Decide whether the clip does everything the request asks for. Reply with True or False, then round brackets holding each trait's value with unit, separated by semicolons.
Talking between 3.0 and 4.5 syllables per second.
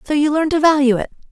False (7.1 syllables/s)